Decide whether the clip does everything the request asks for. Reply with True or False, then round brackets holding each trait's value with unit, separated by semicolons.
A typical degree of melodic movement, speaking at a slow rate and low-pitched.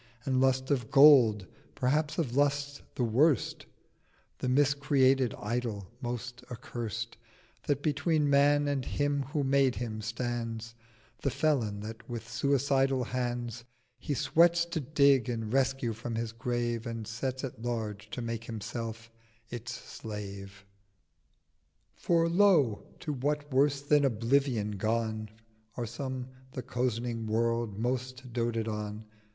True (3.5 semitones; 130 wpm; 125 Hz)